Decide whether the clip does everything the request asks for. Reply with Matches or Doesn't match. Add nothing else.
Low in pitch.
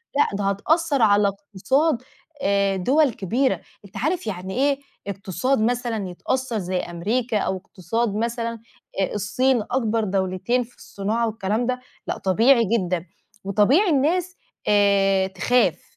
Doesn't match